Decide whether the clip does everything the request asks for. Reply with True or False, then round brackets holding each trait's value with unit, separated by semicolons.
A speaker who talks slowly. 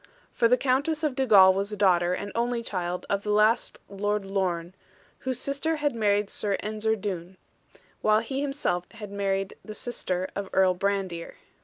False (165 wpm)